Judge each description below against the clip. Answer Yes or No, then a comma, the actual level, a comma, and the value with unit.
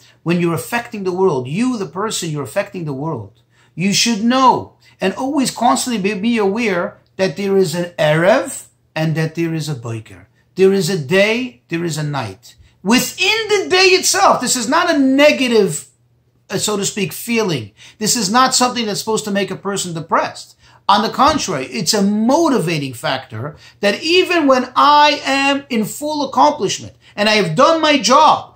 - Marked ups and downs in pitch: Yes, wide, 7.9 semitones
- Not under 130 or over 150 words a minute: No, average, 180 wpm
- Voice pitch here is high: Yes, high, 200 Hz